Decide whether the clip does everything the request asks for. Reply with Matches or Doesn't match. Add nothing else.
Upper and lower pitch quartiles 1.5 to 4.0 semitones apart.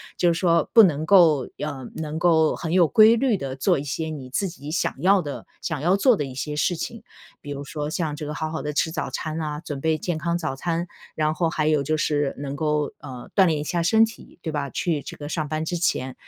Matches